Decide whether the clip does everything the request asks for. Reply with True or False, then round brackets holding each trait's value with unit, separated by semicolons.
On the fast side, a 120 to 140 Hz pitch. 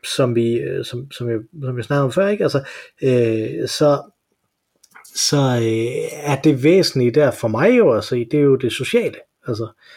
False (170 wpm; 135 Hz)